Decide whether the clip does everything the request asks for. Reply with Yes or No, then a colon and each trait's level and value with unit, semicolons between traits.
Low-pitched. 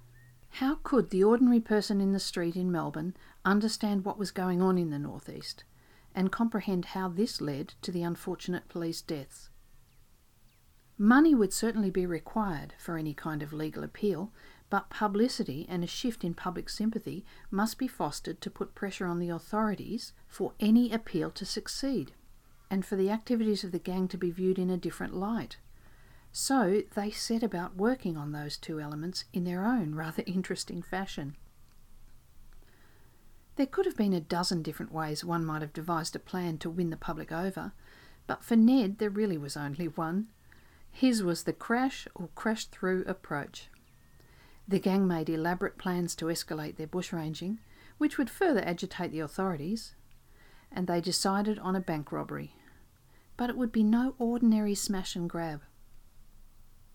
No: medium, 185 Hz